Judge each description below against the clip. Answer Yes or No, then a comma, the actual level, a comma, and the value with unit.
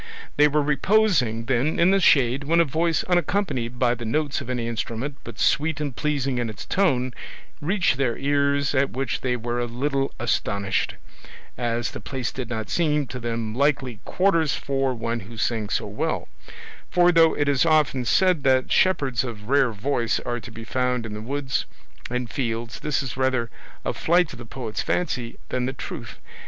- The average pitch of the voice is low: Yes, low, 130 Hz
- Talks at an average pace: Yes, average, 190 wpm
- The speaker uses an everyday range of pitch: Yes, average, 4.0 semitones